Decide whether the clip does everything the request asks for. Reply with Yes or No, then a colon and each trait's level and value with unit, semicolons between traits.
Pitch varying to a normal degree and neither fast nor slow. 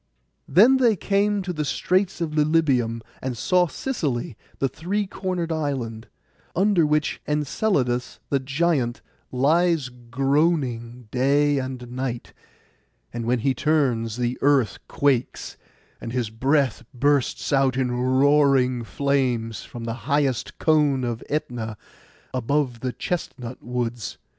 No: average, 3.9 semitones; slow, 125 wpm